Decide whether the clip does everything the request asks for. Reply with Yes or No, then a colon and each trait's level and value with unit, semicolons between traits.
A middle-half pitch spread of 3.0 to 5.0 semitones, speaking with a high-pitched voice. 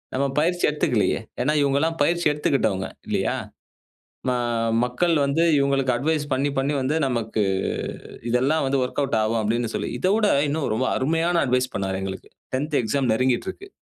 No: average, 4.0 semitones; low, 135 Hz